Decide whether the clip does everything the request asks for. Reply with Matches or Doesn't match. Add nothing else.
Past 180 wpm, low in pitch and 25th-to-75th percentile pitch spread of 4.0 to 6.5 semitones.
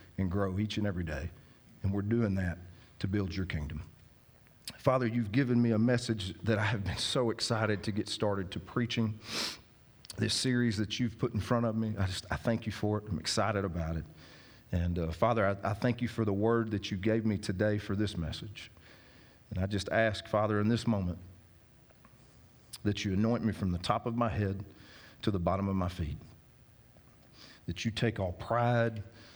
Doesn't match